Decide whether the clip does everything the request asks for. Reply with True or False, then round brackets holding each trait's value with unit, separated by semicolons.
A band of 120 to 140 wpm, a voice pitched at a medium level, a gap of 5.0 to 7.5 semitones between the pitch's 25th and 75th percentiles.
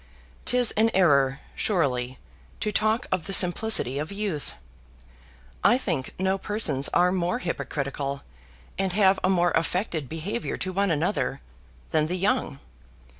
True (135 wpm; 180 Hz; 5.3 semitones)